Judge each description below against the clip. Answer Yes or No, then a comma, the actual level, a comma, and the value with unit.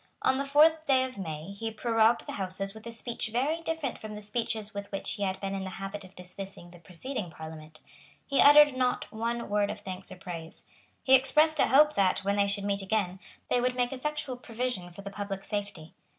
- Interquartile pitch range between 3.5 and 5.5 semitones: Yes, average, 4.7 semitones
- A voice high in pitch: Yes, high, 210 Hz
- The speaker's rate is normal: No, fast, 220 wpm